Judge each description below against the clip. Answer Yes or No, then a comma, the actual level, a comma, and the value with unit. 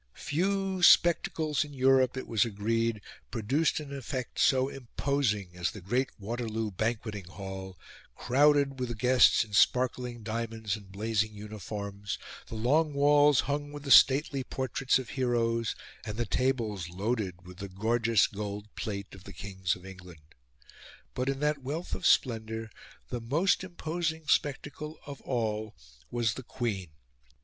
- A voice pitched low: Yes, low, 115 Hz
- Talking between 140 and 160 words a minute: Yes, average, 145 wpm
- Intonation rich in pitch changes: No, average, 4.9 semitones